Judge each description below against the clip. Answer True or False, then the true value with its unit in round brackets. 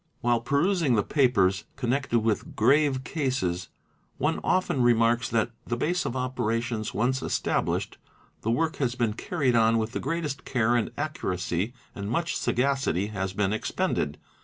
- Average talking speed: True (150 wpm)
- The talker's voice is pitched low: True (120 Hz)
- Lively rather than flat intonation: False (4.1 semitones)